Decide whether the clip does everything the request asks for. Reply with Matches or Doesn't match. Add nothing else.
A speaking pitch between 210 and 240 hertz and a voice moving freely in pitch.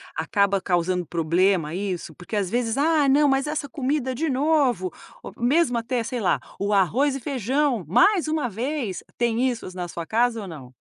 Matches